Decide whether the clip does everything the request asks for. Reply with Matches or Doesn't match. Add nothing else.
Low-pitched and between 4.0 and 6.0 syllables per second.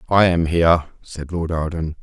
Matches